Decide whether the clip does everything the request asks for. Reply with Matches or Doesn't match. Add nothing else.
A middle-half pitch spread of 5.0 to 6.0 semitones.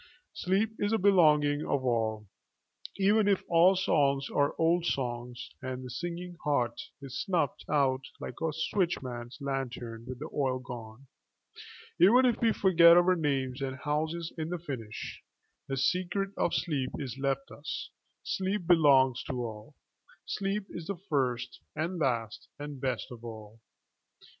Matches